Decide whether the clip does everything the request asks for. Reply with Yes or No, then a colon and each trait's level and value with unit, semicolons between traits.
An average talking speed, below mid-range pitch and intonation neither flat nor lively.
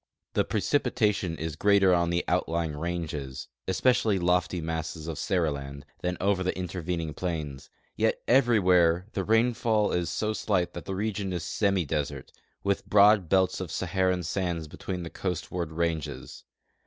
Yes: average, 145 wpm; very low, 90 Hz; average, 3.3 semitones